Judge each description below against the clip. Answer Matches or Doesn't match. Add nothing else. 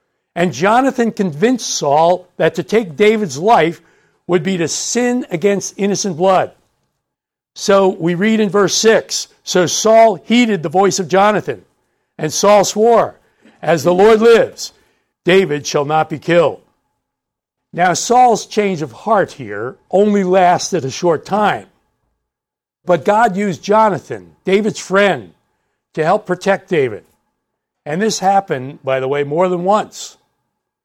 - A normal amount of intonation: Matches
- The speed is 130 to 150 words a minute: Matches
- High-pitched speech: Matches